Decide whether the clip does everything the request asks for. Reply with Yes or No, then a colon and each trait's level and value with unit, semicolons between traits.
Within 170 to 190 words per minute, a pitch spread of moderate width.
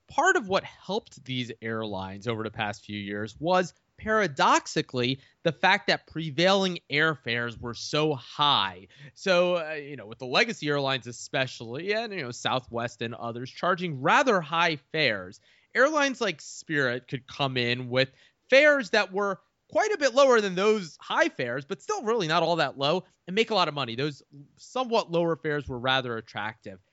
No: average, 175 wpm; wide, 7.7 semitones